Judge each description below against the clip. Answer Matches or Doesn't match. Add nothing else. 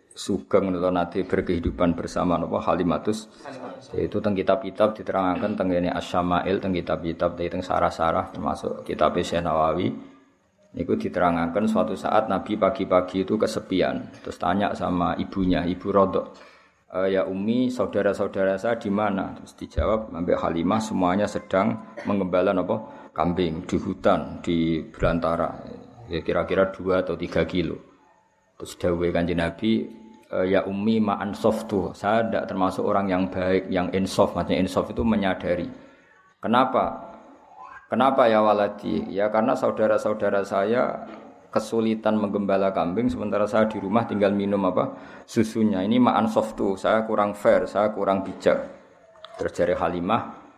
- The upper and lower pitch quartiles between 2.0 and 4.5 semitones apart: Matches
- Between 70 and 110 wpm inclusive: Doesn't match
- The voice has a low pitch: Matches